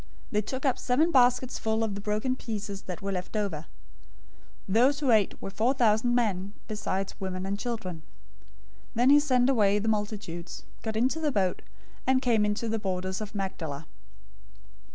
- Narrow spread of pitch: No, average, 4.0 semitones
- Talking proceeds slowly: No, average, 175 wpm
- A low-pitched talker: No, high, 215 Hz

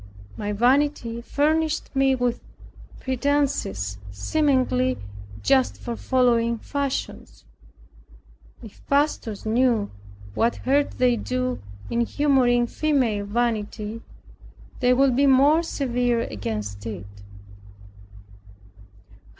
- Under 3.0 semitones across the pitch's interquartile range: No, average, 4.3 semitones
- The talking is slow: Yes, slow, 90 wpm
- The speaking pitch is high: Yes, high, 245 Hz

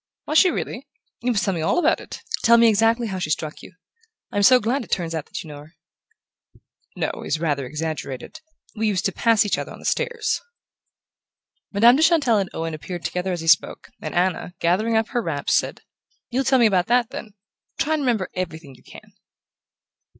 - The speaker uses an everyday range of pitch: No, wide, 6.3 semitones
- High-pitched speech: Yes, high, 200 Hz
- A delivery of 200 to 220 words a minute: Yes, fast, 205 wpm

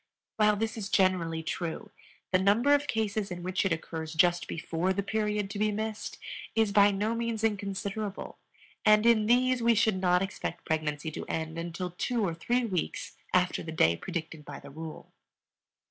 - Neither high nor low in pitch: No, high, 195 Hz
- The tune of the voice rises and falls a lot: No, average, 4.4 semitones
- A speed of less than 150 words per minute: No, average, 175 wpm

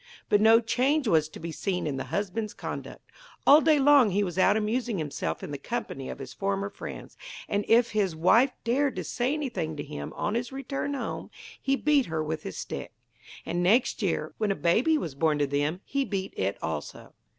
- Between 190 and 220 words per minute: Yes, fast, 205 wpm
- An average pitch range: No, wide, 7.9 semitones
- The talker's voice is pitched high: Yes, high, 205 Hz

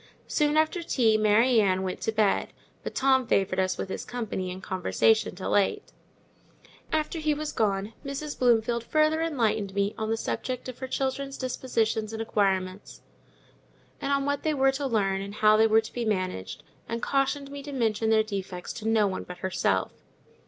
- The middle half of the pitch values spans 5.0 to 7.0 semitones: Yes, average, 5.3 semitones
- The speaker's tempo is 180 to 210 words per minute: Yes, average, 185 wpm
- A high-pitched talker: Yes, high, 225 Hz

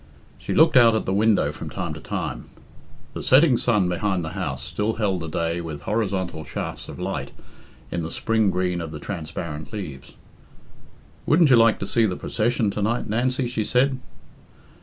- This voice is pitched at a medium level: No, low, 100 Hz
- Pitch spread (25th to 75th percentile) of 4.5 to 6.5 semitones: Yes, wide, 5.6 semitones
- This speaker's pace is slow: No, average, 180 wpm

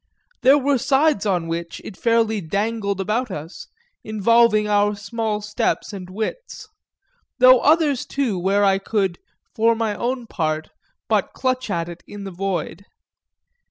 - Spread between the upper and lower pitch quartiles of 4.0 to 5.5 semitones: No, average, 3.5 semitones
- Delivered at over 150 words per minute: No, average, 145 wpm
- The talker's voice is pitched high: Yes, high, 210 Hz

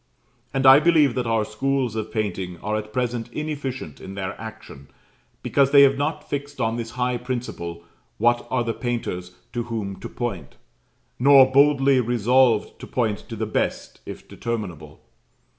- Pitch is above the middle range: No, low, 120 Hz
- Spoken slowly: No, average, 160 wpm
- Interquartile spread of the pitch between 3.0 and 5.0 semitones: Yes, average, 3.8 semitones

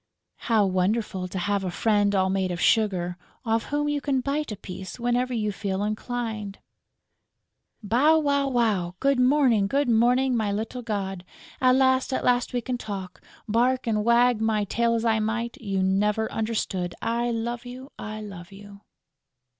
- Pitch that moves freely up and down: No, average, 3.6 semitones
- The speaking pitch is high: Yes, high, 225 Hz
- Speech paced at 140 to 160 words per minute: No, average, 170 wpm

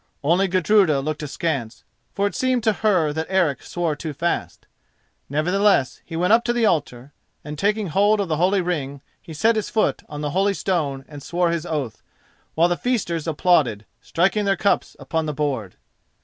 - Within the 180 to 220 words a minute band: Yes, average, 185 wpm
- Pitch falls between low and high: Yes, medium, 170 Hz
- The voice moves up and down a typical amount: Yes, average, 4.9 semitones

